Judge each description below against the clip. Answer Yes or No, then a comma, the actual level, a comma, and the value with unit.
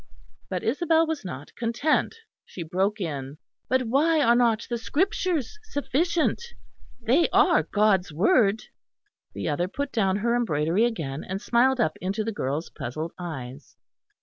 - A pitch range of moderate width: No, wide, 8.1 semitones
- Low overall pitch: No, high, 225 Hz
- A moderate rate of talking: Yes, average, 145 wpm